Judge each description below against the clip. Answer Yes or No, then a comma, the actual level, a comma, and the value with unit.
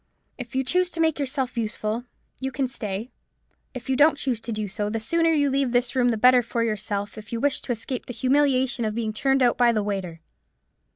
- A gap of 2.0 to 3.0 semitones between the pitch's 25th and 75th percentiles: No, average, 3.7 semitones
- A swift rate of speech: Yes, fast, 225 wpm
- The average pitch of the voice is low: No, high, 245 Hz